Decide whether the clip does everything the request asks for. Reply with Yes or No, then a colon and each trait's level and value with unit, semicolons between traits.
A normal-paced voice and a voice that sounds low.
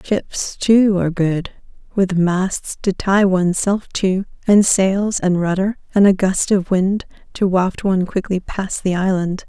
No: average, 170 wpm; high, 190 Hz